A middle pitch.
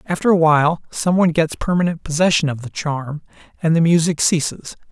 Yes: medium, 160 Hz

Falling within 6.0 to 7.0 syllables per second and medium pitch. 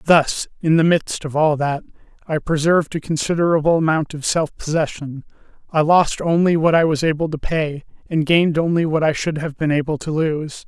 No: 5.2 syllables/s; medium, 155 Hz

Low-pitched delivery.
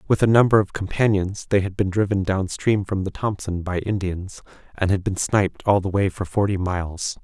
Yes: low, 100 Hz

